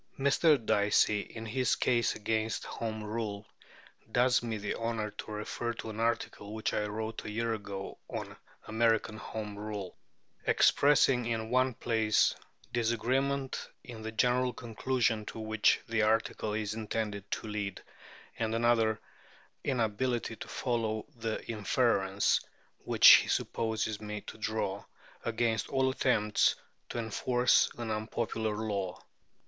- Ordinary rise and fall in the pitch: No, narrow, 1.9 semitones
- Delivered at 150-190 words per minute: No, slow, 135 wpm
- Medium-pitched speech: No, low, 110 Hz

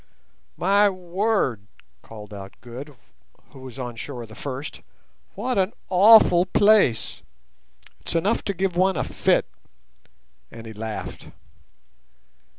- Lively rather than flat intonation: Yes, wide, 9.0 semitones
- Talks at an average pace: No, slow, 120 wpm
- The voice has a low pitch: No, medium, 155 Hz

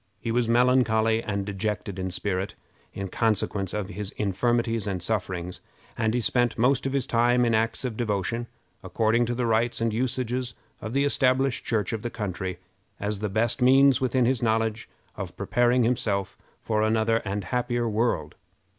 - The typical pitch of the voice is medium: No, low, 115 Hz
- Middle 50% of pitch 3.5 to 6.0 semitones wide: No, average, 2.8 semitones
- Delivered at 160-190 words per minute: Yes, average, 170 wpm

